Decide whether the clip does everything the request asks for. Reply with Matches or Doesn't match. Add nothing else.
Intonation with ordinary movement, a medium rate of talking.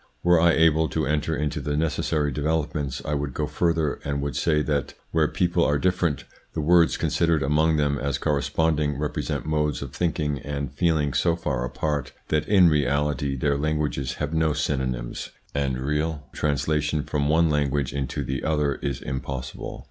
Doesn't match